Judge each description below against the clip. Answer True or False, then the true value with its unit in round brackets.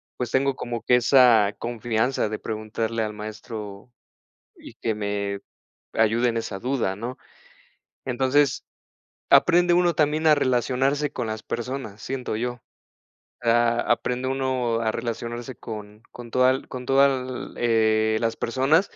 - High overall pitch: False (120 Hz)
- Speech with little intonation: False (3.0 semitones)